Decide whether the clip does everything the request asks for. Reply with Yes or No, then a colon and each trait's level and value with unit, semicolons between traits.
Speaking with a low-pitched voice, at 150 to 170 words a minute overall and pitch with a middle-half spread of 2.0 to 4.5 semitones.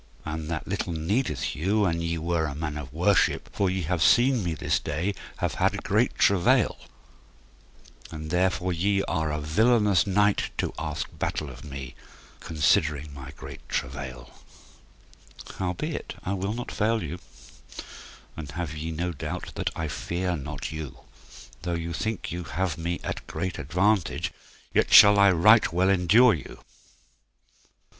Yes: very low, 85 Hz; average, 155 wpm; average, 4.1 semitones